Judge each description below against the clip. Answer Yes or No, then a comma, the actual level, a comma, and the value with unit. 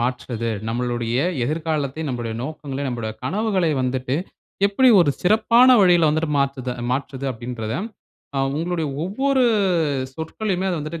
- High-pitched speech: No, medium, 145 Hz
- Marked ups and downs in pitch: Yes, wide, 6.1 semitones